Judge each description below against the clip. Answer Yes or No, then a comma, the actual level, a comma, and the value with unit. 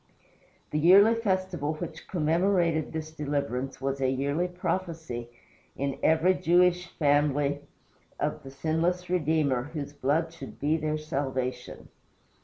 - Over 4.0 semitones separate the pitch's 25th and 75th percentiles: No, average, 3.7 semitones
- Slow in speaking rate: Yes, slow, 120 wpm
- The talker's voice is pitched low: No, medium, 155 Hz